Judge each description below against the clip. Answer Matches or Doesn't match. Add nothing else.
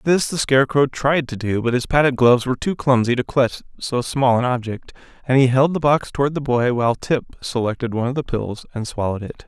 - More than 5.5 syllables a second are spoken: Matches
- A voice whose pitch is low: Matches